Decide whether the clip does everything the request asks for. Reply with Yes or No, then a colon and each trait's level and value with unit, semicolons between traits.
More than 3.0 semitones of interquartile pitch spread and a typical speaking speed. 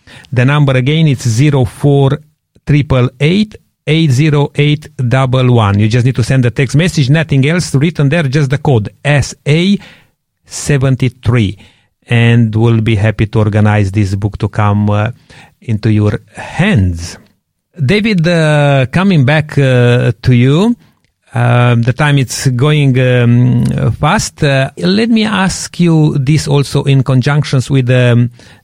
Yes: average, 4.0 semitones; average, 150 wpm